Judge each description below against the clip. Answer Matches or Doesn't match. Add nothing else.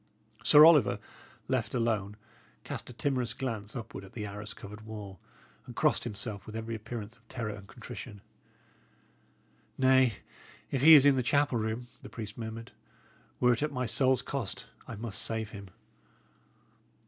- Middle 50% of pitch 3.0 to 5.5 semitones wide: Matches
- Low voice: Matches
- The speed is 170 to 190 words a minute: Doesn't match